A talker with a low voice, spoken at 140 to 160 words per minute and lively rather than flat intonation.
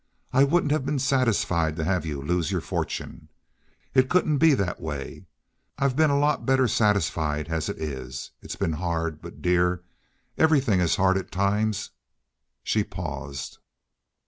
Yes: very low, 95 Hz; average, 155 wpm; wide, 8.7 semitones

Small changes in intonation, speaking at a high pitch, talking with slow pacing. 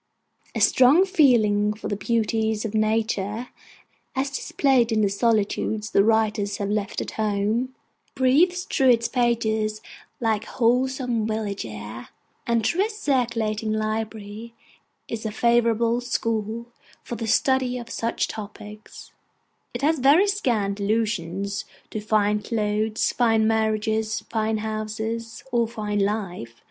Yes: narrow, 2.1 semitones; high, 220 Hz; slow, 130 wpm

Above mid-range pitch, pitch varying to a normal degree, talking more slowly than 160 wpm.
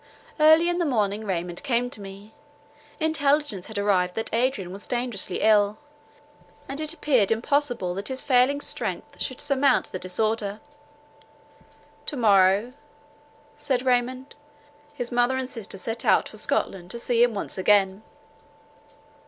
Yes: high, 235 Hz; average, 4.8 semitones; average, 140 wpm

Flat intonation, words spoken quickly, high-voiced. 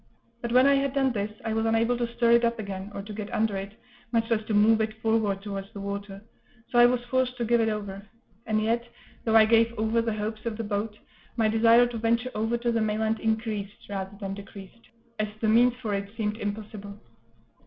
Yes: narrow, 2.1 semitones; fast, 225 wpm; high, 220 Hz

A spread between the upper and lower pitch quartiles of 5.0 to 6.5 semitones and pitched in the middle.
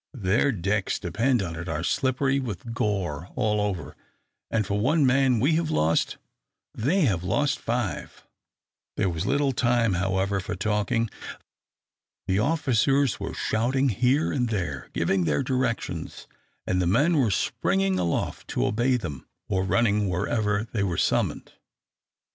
No: wide, 5.6 semitones; low, 105 Hz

